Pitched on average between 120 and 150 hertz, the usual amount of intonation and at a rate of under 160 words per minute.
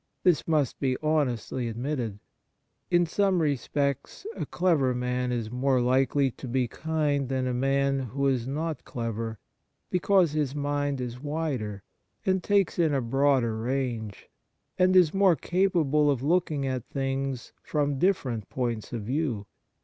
Yes: low, 135 Hz; average, 3.8 semitones; average, 150 wpm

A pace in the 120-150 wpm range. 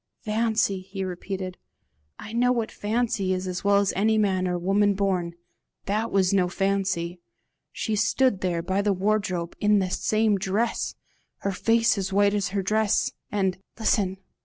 No: average, 160 wpm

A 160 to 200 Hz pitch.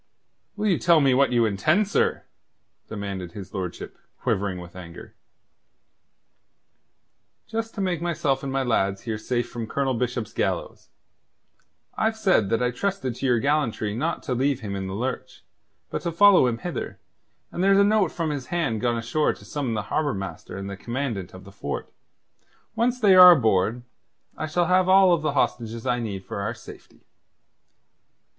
No: low, 125 Hz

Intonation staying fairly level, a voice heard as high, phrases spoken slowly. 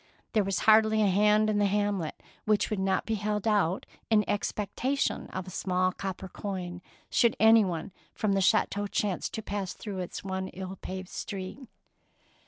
No: narrow, 2.1 semitones; high, 200 Hz; average, 170 wpm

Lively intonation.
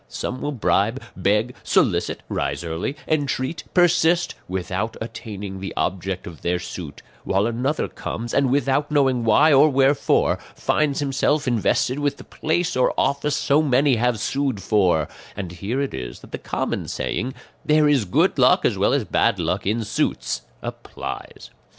Yes: wide, 6.3 semitones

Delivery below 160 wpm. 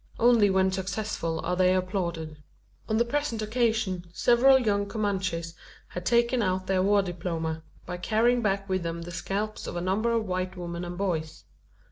No: average, 170 wpm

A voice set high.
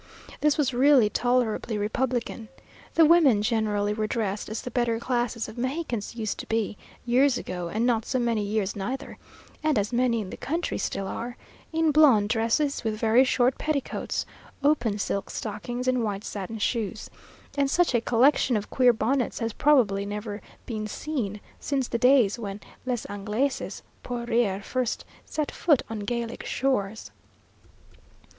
Yes: high, 235 Hz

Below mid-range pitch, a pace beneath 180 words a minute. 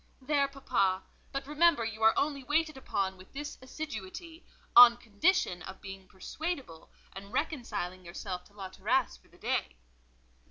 No: high, 235 Hz; average, 150 wpm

